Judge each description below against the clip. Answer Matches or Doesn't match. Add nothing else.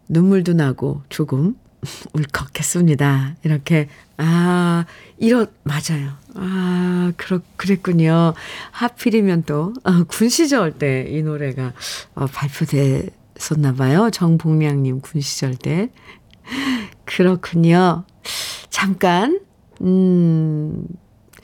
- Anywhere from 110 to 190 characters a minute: Matches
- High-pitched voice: Doesn't match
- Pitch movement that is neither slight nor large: Matches